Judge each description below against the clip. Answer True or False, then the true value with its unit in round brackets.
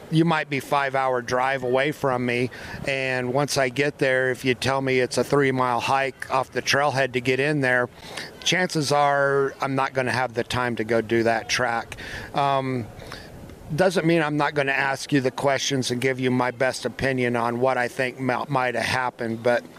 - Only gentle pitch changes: True (2.0 semitones)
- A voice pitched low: True (130 Hz)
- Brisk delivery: True (210 wpm)